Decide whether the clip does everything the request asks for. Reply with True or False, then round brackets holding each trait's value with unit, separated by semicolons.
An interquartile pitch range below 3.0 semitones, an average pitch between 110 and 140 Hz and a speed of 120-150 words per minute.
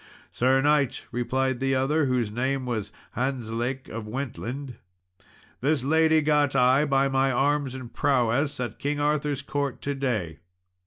True (2.6 semitones; 135 Hz; 145 wpm)